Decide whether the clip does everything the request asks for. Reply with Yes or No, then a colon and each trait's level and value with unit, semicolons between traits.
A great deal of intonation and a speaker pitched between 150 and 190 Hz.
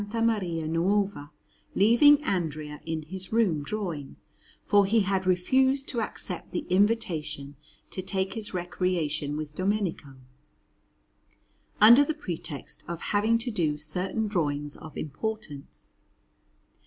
Yes: wide, 5.7 semitones; medium, 185 Hz